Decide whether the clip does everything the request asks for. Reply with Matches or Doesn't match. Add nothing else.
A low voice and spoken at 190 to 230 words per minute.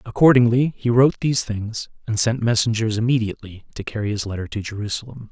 Doesn't match